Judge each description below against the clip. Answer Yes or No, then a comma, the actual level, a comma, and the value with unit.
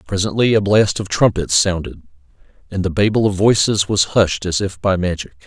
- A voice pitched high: No, very low, 95 Hz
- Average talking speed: Yes, average, 185 wpm